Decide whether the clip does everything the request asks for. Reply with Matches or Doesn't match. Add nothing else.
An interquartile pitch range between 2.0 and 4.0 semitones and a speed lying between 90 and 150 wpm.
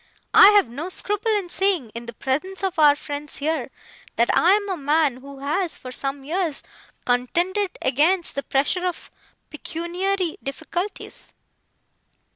Doesn't match